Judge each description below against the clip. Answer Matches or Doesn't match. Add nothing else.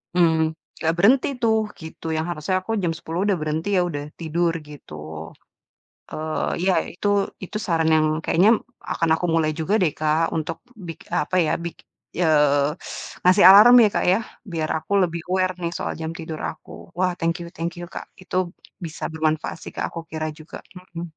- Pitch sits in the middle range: Matches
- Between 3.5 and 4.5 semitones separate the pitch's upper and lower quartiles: Doesn't match